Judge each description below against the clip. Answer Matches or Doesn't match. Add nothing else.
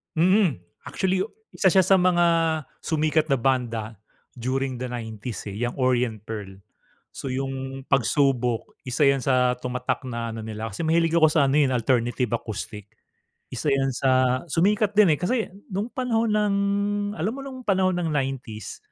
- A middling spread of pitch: Doesn't match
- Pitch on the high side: Doesn't match